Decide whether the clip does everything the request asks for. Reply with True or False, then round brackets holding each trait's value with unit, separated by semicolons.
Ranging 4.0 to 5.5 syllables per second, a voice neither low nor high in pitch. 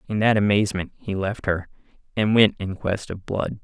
False (5.1 syllables/s; 100 Hz)